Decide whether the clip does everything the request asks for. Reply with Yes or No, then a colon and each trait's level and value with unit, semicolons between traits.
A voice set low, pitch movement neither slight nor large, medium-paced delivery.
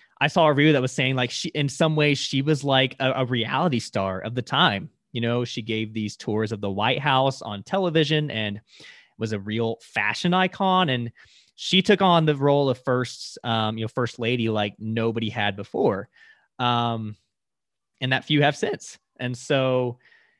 Yes: low, 125 Hz; average, 4.5 semitones; average, 190 wpm